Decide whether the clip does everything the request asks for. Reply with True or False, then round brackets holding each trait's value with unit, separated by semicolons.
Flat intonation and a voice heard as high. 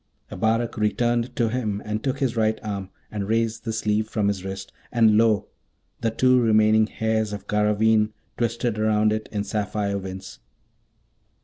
False (1.5 semitones; 110 Hz)